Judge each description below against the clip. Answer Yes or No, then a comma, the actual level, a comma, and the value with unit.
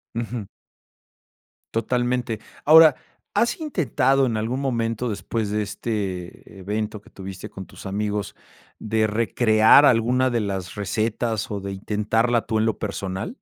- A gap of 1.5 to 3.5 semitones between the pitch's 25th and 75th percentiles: Yes, average, 2.9 semitones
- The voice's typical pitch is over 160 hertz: No, low, 110 Hz